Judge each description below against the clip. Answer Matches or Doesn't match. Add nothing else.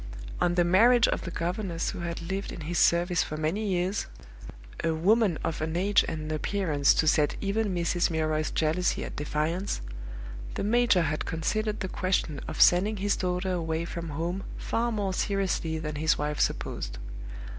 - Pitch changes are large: Doesn't match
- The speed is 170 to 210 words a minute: Matches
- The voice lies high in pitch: Doesn't match